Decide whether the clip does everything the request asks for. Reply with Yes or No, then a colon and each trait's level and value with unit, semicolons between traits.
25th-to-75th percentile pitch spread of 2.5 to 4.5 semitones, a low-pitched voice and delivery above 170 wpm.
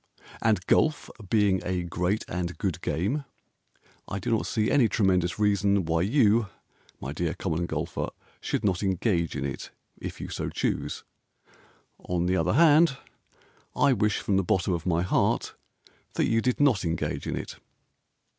No: average, 4.2 semitones; very low, 95 Hz; average, 160 wpm